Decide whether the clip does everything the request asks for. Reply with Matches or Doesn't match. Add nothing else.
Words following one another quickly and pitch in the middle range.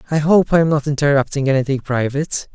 Doesn't match